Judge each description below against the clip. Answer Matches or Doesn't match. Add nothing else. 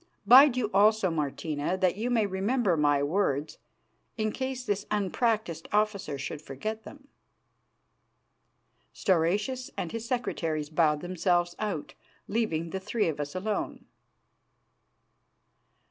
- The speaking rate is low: Matches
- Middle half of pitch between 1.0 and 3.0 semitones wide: Doesn't match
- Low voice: Doesn't match